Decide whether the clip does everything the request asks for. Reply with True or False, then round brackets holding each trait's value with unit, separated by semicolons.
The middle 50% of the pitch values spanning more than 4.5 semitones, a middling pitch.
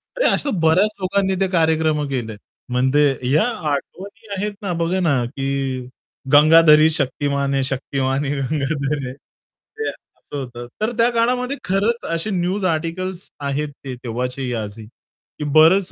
True (5.6 semitones; 155 Hz)